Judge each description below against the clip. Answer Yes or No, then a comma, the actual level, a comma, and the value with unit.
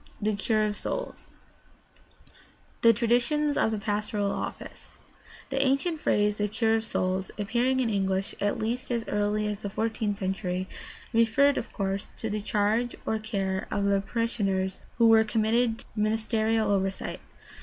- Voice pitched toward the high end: Yes, high, 215 Hz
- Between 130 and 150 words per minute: No, average, 160 wpm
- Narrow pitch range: Yes, narrow, 2.3 semitones